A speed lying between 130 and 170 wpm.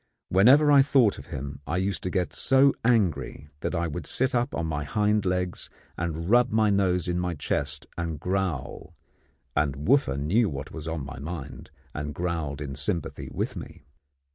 No: average, 180 wpm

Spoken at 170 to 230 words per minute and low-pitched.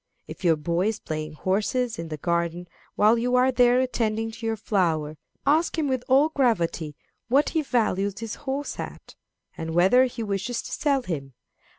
No: average, 180 wpm; high, 220 Hz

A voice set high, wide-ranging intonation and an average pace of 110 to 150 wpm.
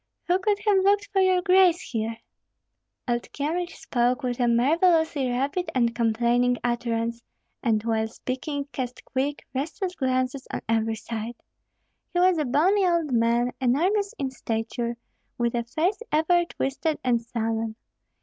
Yes: very high, 260 Hz; wide, 6.4 semitones; average, 145 wpm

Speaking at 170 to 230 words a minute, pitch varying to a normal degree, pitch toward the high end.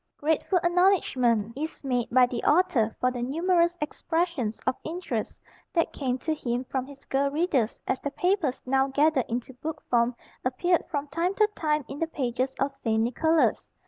Yes: average, 175 wpm; average, 4.7 semitones; very high, 275 Hz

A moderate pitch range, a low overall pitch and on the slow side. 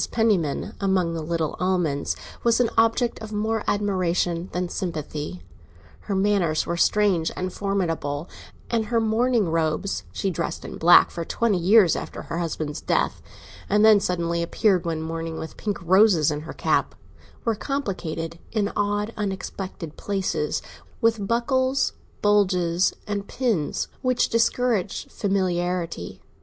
No: average, 4.3 semitones; high, 190 Hz; slow, 130 wpm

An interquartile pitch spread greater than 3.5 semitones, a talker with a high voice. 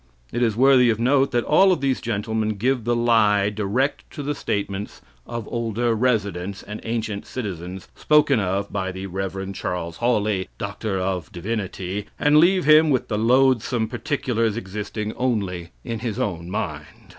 No: average, 4.0 semitones; low, 110 Hz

